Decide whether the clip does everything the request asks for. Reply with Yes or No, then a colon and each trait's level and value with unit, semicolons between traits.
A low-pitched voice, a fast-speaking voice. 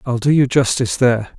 Yes: low, 125 Hz; fast, 215 wpm